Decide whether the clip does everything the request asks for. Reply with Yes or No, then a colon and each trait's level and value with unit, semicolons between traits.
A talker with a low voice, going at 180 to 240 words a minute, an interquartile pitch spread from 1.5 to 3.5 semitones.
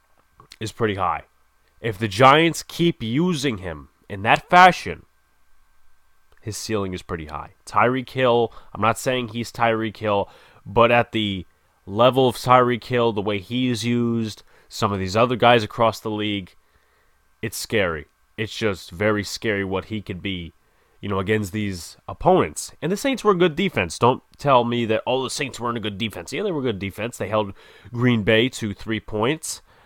No: low, 110 Hz; average, 185 wpm; average, 4.1 semitones